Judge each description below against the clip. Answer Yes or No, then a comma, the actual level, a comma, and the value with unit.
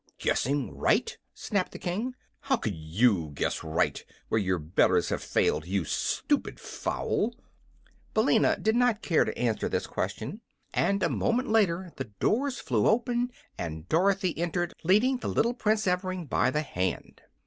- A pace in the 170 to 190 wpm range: No, average, 155 wpm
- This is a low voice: No, medium, 180 Hz